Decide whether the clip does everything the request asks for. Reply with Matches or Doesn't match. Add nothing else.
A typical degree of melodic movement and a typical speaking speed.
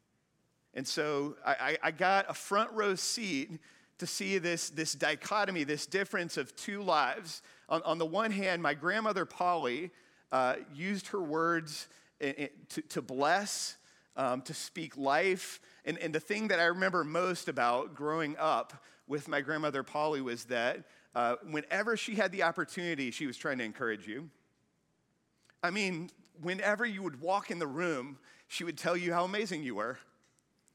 Matches